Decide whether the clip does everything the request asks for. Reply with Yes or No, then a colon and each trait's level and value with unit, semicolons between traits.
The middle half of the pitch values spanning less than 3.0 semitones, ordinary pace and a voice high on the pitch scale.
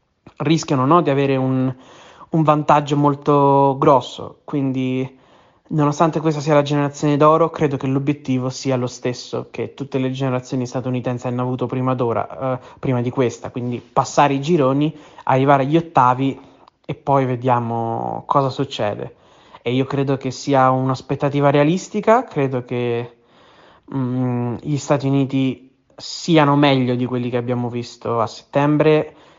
No: narrow, 2.4 semitones; average, 140 wpm; low, 135 Hz